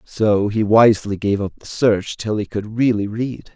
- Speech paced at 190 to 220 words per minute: Yes, fast, 205 wpm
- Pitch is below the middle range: Yes, low, 105 Hz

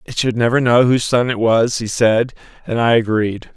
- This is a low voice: Yes, low, 115 Hz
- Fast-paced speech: Yes, fast, 220 wpm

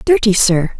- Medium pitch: No, high, 220 Hz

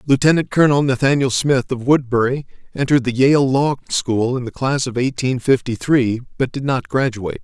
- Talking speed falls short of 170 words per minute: No, average, 180 wpm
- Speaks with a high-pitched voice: No, low, 130 Hz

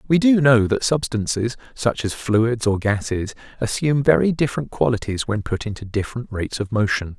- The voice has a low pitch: Yes, low, 115 Hz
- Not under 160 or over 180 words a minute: Yes, average, 175 wpm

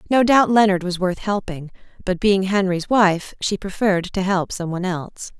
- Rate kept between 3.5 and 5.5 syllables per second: Yes, 5.0 syllables/s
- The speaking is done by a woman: Yes, female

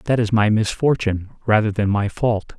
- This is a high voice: No, low, 110 Hz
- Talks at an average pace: Yes, average, 185 wpm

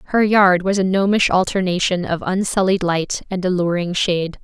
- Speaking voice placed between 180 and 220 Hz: Yes, medium, 185 Hz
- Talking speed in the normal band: Yes, average, 160 wpm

